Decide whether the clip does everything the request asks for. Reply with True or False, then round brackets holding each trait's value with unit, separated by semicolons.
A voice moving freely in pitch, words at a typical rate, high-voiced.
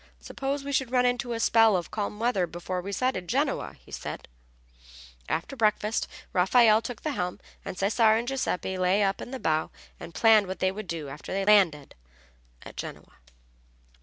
False (4.7 semitones; 180 wpm; 210 Hz)